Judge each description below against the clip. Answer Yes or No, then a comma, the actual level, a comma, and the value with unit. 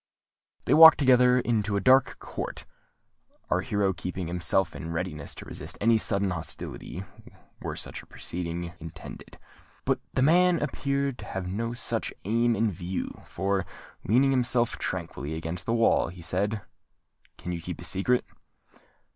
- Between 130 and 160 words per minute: Yes, average, 150 wpm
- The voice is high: No, low, 100 Hz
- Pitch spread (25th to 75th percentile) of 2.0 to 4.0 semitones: No, wide, 5.5 semitones